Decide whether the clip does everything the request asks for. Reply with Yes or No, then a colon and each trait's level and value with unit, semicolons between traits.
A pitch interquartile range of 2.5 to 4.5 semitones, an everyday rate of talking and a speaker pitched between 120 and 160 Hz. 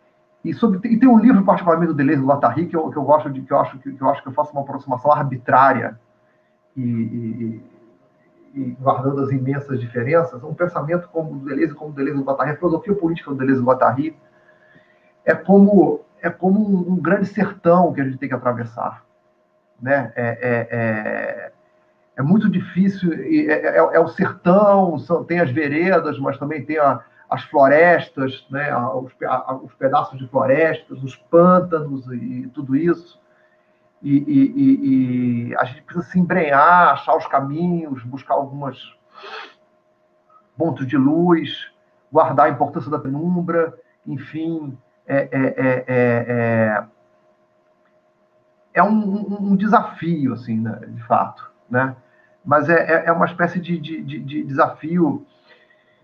No: wide, 5.6 semitones; average, 155 wpm; medium, 140 Hz